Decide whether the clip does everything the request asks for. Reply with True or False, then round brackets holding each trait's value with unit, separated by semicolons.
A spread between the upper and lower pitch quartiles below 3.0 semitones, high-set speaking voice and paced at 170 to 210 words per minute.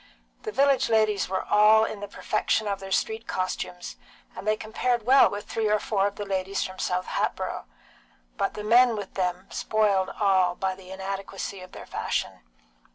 True (2.4 semitones; 200 Hz; 180 wpm)